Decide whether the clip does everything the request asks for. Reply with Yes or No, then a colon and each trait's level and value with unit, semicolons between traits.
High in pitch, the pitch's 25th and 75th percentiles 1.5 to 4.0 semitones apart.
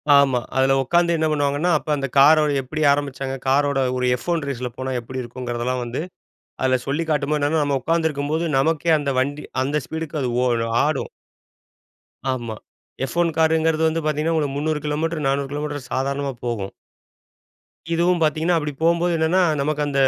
No: medium, 145 Hz; average, 2.9 semitones